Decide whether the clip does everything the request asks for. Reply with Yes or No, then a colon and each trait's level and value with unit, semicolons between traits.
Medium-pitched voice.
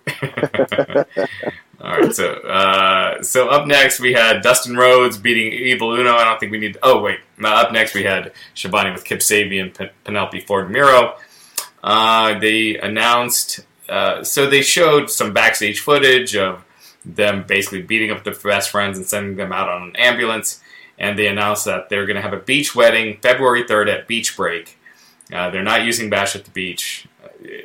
No: low, 110 Hz